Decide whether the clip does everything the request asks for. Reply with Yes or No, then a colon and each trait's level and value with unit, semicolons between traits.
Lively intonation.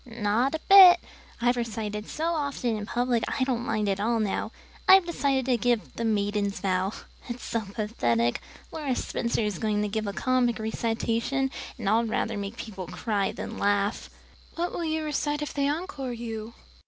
No: average, 4.3 semitones